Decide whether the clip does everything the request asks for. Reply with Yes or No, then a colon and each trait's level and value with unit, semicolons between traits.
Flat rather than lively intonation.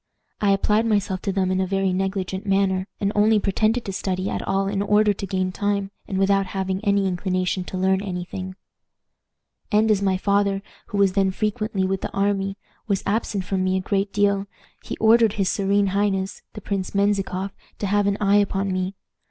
Yes: narrow, 1.2 semitones